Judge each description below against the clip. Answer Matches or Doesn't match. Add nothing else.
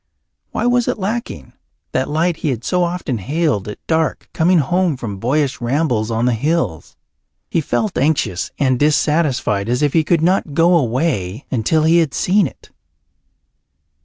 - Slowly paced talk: Doesn't match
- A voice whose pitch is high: Doesn't match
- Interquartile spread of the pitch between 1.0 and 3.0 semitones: Doesn't match